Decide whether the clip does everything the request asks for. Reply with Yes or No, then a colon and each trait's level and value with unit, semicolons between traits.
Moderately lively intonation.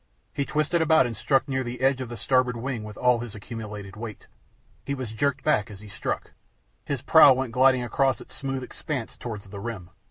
Yes: average, 3.6 semitones